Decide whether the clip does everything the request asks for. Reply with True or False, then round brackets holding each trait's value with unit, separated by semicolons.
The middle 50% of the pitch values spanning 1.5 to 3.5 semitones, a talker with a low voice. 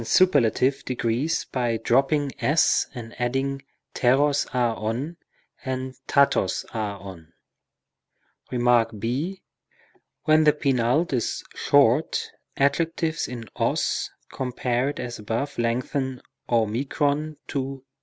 True (3.2 semitones; 130 Hz)